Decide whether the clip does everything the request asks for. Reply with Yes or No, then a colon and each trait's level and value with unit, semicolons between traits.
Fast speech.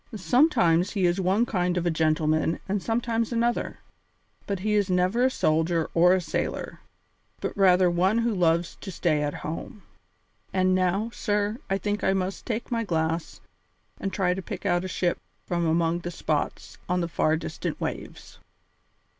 No: average, 170 wpm